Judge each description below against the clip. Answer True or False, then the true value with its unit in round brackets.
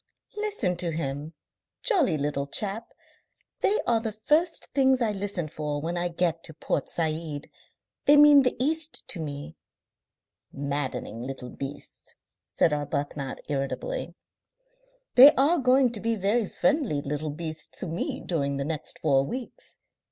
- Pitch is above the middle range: False (170 Hz)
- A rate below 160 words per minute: True (145 wpm)